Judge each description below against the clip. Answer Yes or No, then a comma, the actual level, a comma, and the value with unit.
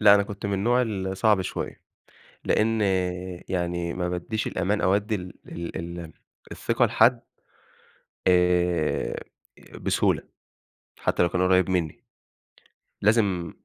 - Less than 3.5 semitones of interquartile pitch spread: Yes, average, 2.7 semitones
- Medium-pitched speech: No, very low, 95 Hz